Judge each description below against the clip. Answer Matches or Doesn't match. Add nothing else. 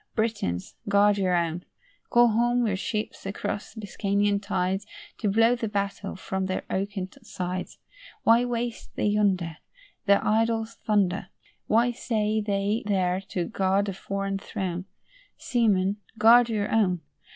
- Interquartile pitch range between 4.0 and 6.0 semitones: Doesn't match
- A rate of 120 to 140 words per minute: Matches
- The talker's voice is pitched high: Matches